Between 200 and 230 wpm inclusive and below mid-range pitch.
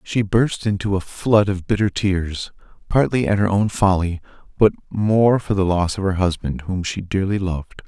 No: average, 190 wpm; very low, 95 Hz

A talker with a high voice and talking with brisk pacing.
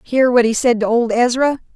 Yes: high, 240 Hz; fast, 240 wpm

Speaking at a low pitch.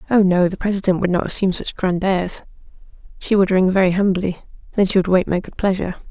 No: medium, 185 Hz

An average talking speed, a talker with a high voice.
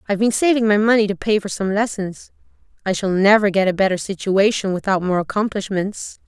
Yes: average, 190 wpm; high, 200 Hz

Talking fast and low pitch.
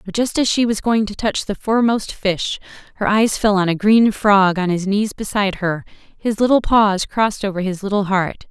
No: fast, 220 wpm; high, 205 Hz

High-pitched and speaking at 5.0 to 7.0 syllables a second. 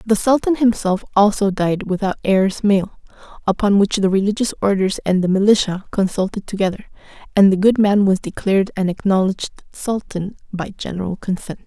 Yes: high, 200 Hz; 5.3 syllables/s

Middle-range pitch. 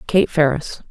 Yes: medium, 160 Hz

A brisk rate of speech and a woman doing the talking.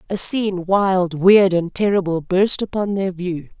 No: average, 165 wpm; female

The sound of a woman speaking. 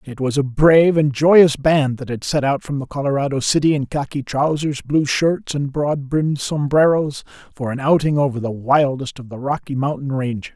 No: male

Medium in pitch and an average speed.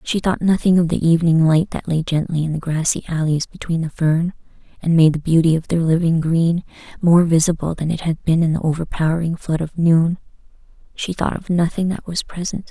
No: medium, 165 Hz; fast, 210 wpm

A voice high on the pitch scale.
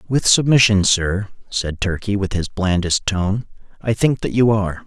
No: low, 100 Hz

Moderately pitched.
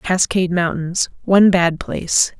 Yes: medium, 175 Hz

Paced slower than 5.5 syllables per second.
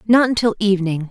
No: 6.6 syllables/s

